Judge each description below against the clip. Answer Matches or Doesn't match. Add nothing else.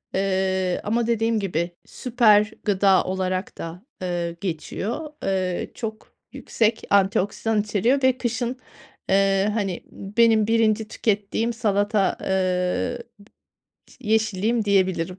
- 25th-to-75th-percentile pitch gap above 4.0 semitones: Doesn't match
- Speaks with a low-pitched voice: Doesn't match